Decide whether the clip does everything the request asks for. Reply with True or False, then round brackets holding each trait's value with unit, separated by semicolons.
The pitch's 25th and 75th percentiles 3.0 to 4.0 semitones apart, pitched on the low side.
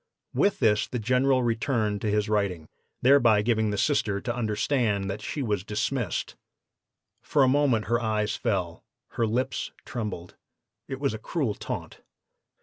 True (3.6 semitones; 110 Hz)